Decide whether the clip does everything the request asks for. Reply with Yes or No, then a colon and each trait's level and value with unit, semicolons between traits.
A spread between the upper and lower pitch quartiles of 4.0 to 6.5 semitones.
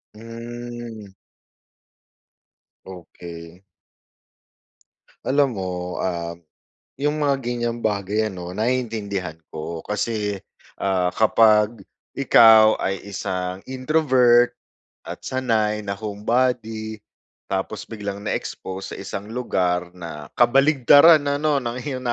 Yes: average, 4.3 semitones